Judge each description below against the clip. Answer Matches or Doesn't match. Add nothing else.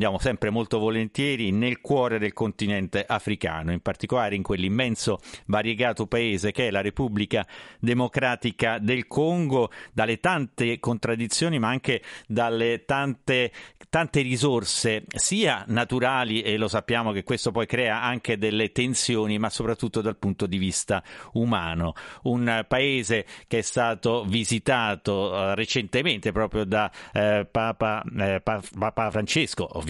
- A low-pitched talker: Matches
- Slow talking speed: Doesn't match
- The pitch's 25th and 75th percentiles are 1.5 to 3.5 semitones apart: Matches